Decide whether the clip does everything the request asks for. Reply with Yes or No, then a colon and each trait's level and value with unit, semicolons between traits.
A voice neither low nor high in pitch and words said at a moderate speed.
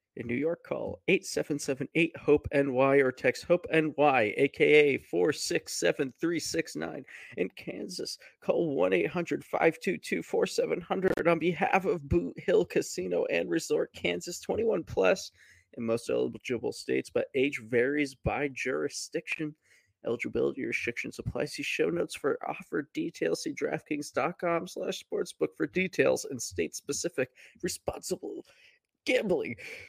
No: medium, 170 Hz; slow, 110 wpm